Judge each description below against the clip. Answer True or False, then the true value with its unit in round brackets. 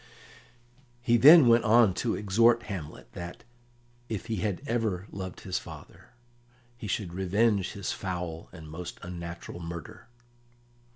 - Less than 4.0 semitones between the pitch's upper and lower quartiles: False (4.7 semitones)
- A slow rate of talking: True (130 wpm)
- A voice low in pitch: True (95 Hz)